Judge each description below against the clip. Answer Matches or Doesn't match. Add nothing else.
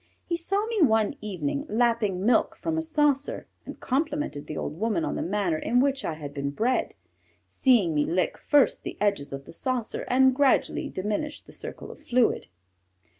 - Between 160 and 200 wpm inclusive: Matches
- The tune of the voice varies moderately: Doesn't match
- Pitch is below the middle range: Doesn't match